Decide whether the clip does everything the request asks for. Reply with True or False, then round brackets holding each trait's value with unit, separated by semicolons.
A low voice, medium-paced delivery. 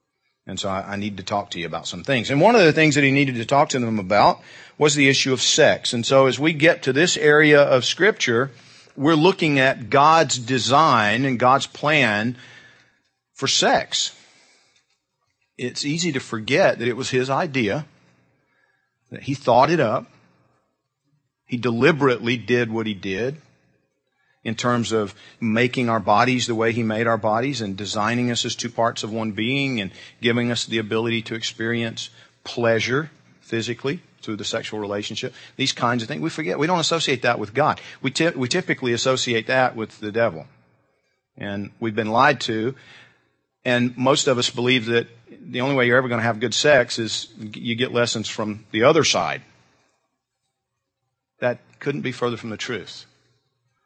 True (120 Hz; 175 wpm)